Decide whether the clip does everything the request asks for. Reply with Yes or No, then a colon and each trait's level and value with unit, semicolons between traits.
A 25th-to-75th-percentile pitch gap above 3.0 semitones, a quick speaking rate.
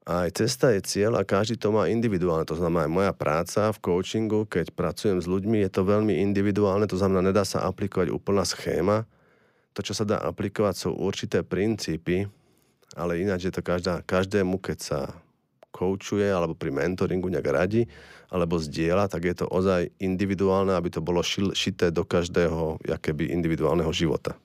No: average, 2.7 semitones; fast, 170 wpm